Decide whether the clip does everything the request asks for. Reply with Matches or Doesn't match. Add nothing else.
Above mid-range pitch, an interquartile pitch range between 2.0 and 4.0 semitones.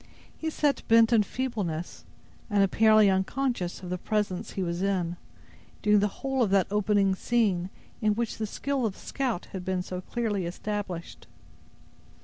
Matches